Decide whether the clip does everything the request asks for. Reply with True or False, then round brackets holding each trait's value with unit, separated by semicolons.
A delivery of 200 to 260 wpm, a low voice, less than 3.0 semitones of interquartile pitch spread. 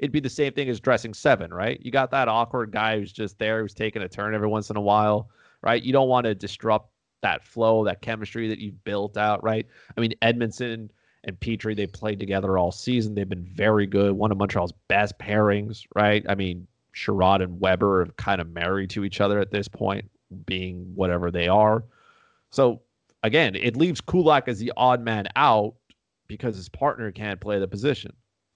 True (205 wpm; 105 Hz; 2.4 semitones)